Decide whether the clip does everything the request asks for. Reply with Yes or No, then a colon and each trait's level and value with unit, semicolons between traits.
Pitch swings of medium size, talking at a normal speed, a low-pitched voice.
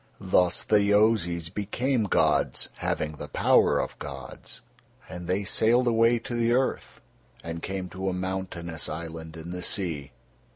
Yes: average, 4.7 semitones; average, 150 wpm; very low, 95 Hz